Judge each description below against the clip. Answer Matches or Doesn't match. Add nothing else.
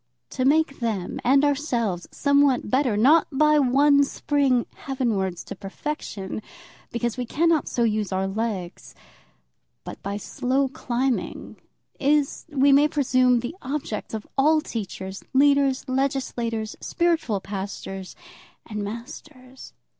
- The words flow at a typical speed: Doesn't match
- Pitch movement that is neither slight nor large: Matches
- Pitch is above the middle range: Matches